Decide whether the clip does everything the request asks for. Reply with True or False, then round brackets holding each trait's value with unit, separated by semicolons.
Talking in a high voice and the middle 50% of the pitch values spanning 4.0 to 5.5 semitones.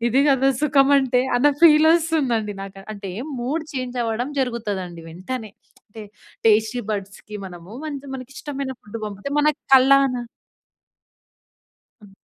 True (245 Hz; 4.8 semitones)